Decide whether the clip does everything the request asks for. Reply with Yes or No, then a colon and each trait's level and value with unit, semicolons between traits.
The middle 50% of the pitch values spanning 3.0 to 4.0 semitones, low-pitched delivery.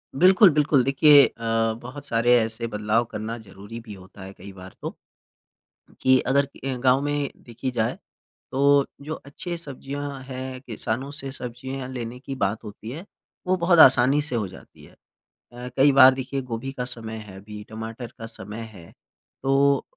Yes: average, 3.7 semitones; low, 130 Hz